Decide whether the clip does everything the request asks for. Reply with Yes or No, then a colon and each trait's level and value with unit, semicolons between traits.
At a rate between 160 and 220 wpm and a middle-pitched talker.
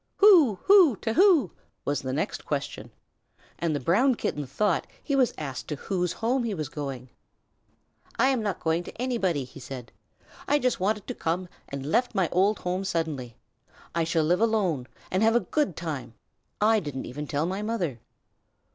Yes: average, 180 wpm; medium, 180 Hz